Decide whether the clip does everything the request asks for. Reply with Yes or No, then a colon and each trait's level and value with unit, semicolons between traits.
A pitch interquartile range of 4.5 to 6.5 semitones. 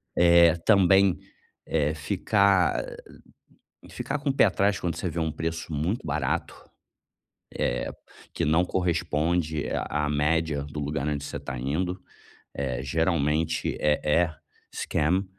No: average, 3.1 semitones